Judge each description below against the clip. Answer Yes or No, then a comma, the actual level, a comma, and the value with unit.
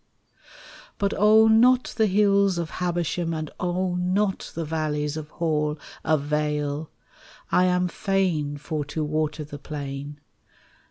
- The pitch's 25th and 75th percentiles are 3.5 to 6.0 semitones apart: Yes, average, 3.8 semitones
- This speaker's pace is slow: Yes, slow, 125 wpm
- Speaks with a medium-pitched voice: Yes, medium, 160 Hz